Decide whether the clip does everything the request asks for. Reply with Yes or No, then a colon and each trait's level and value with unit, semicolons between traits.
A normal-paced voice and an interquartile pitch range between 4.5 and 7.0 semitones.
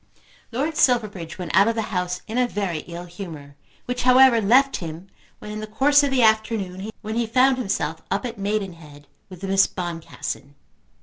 Yes: average, 175 wpm; average, 5.1 semitones